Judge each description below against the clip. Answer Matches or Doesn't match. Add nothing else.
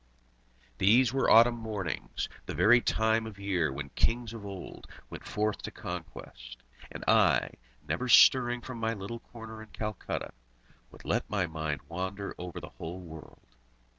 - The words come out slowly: Doesn't match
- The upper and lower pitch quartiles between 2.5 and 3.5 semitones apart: Doesn't match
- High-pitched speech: Doesn't match